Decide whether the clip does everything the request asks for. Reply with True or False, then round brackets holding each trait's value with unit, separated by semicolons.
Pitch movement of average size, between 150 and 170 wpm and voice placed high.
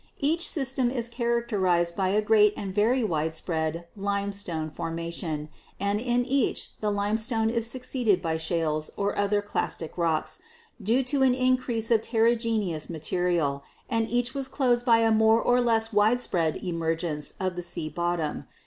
False (5.7 semitones; 155 wpm; 210 Hz)